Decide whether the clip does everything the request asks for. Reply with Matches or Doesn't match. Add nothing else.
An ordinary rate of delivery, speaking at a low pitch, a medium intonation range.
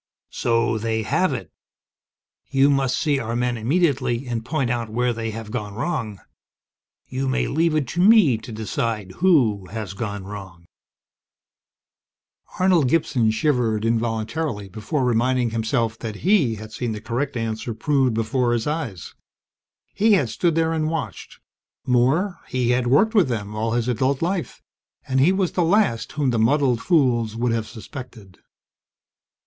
Matches